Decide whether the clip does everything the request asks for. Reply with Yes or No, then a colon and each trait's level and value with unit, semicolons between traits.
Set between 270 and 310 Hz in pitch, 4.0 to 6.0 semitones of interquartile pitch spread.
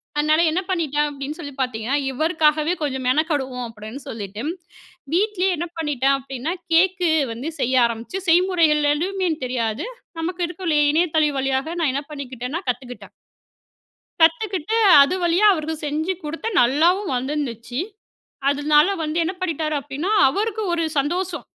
Yes: very high, 300 Hz; average, 4.5 semitones